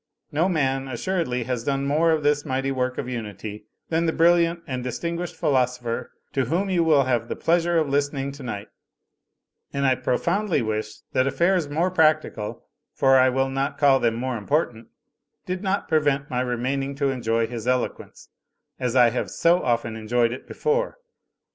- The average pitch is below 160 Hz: Yes, low, 135 Hz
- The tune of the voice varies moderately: Yes, average, 4.6 semitones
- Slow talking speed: No, average, 170 wpm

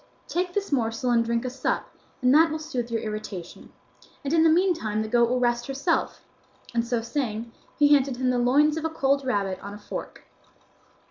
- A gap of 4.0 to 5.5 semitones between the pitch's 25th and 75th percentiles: Yes, average, 4.3 semitones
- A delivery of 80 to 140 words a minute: No, average, 200 wpm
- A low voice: No, very high, 250 Hz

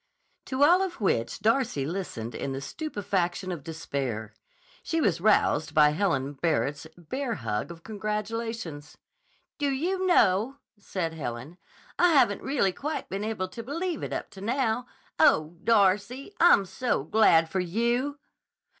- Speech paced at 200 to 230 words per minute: No, average, 145 wpm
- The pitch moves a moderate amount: No, wide, 7.7 semitones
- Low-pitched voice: No, high, 200 Hz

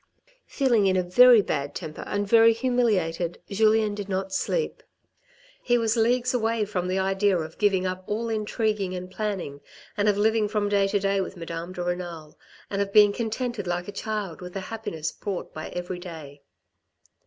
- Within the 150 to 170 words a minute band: No, average, 180 wpm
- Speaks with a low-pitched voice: No, high, 200 Hz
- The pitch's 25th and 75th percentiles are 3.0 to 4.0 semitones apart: Yes, average, 3.5 semitones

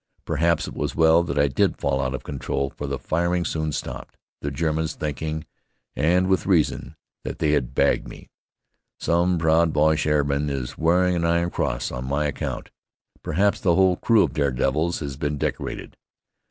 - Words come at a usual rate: Yes, average, 180 wpm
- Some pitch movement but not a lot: Yes, average, 3.0 semitones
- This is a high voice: No, very low, 80 Hz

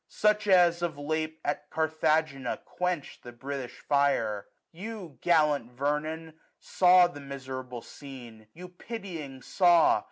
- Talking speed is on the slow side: Yes, slow, 125 wpm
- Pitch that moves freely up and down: No, average, 4.3 semitones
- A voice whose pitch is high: No, medium, 155 Hz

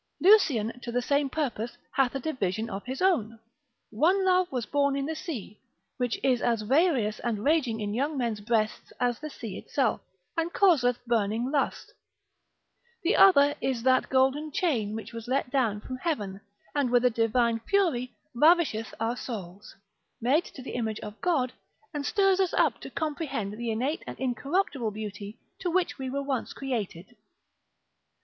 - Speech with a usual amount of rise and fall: Yes, average, 4.7 semitones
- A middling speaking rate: Yes, average, 170 wpm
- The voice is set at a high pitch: Yes, very high, 255 Hz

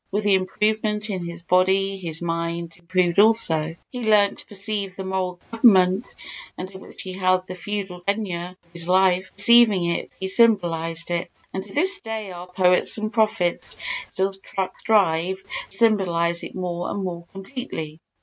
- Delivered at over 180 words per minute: No, average, 160 wpm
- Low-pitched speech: No, high, 190 Hz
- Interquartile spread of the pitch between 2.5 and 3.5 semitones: Yes, average, 3.1 semitones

